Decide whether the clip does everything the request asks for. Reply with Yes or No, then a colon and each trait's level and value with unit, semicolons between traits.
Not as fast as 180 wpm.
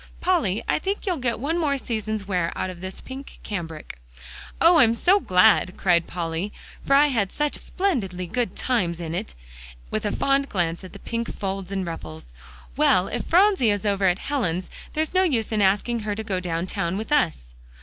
No: average, 200 wpm